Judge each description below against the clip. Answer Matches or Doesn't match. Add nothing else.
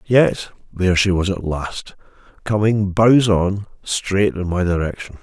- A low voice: Matches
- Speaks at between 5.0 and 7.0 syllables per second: Doesn't match